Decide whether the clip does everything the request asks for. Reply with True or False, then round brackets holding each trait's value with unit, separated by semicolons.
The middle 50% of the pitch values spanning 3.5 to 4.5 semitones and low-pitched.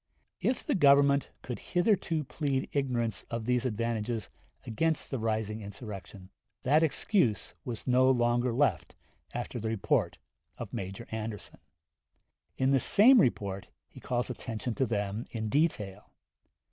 True (4.2 semitones; 120 Hz)